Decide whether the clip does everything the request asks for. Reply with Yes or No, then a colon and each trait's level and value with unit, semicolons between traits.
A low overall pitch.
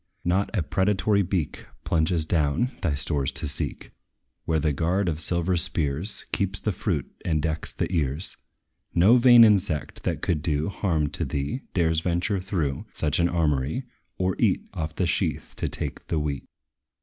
Yes: very low, 85 Hz